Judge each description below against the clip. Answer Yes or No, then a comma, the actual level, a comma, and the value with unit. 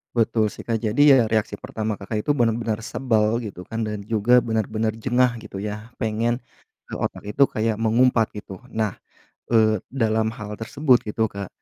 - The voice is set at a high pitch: No, low, 110 Hz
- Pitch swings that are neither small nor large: No, narrow, 1.8 semitones